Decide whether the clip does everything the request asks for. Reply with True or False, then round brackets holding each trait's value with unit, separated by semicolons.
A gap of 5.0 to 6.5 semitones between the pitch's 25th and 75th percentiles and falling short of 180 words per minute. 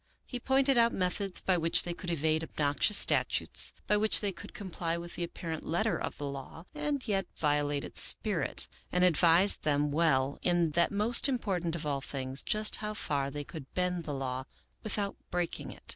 False (5.4 semitones; 190 wpm)